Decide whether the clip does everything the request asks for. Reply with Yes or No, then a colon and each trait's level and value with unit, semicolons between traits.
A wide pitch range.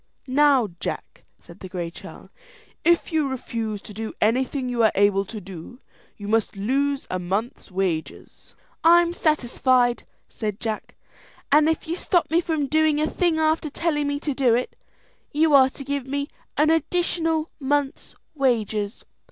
Yes: wide, 5.9 semitones